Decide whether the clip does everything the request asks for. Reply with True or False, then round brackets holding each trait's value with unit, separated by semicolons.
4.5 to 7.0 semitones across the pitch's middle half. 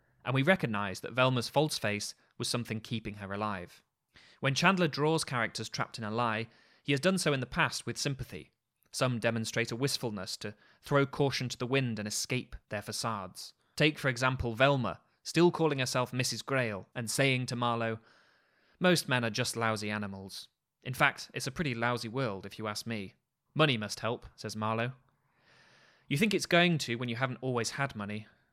False (3.7 semitones)